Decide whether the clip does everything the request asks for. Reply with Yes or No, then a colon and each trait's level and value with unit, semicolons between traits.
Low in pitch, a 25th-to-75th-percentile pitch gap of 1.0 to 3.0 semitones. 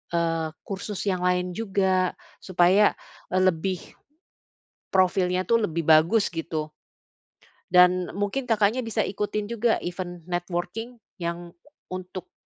No: medium, 185 Hz; average, 2.7 semitones